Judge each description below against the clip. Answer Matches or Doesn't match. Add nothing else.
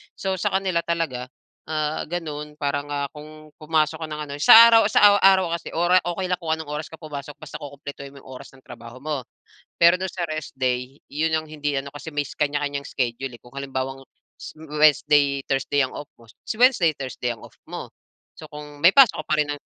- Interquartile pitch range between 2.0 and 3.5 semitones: Matches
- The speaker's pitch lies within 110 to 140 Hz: Doesn't match